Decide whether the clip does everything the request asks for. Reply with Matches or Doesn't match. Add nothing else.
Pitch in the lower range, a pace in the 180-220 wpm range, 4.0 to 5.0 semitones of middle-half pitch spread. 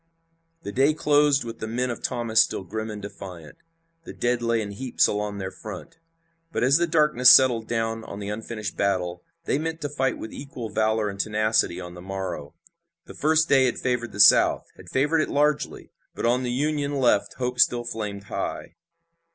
Matches